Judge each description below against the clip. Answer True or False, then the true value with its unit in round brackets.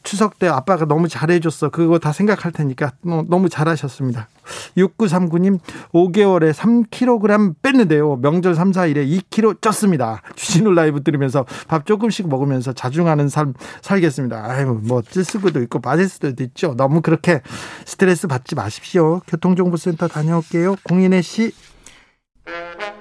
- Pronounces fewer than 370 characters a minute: True (315 characters per minute)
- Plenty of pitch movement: False (4.1 semitones)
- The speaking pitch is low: False (170 Hz)